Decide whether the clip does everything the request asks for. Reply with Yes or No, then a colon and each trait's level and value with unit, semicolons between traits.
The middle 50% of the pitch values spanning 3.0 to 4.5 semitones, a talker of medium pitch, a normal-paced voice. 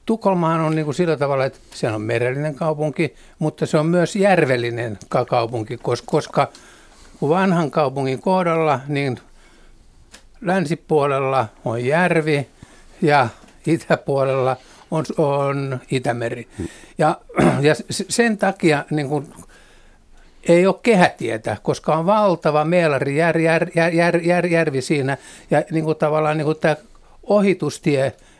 Yes: average, 3.8 semitones; medium, 155 Hz; average, 130 wpm